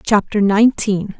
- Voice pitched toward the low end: No, high, 205 Hz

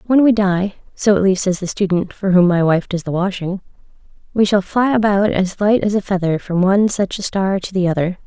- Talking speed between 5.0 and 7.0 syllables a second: Yes, 5.5 syllables/s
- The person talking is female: Yes, female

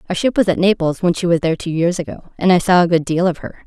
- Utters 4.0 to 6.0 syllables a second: No, 7.0 syllables/s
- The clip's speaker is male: No, female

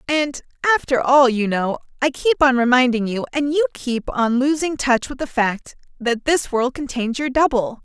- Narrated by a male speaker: No, female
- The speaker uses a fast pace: No, average, 185 wpm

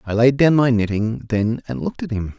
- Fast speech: Yes, fast, 250 wpm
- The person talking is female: No, male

